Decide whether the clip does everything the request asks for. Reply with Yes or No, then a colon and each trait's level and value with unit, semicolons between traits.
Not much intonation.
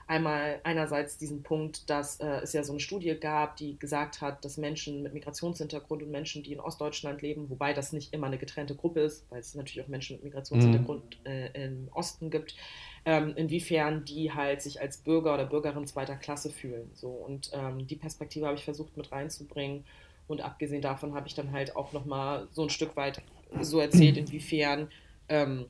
Yes: narrow, 1.5 semitones